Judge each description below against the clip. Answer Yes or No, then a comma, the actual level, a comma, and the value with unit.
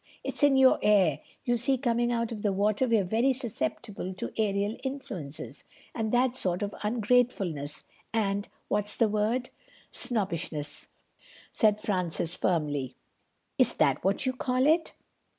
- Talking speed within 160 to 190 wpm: No, slow, 135 wpm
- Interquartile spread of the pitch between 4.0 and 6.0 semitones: Yes, average, 4.6 semitones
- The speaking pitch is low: No, high, 215 Hz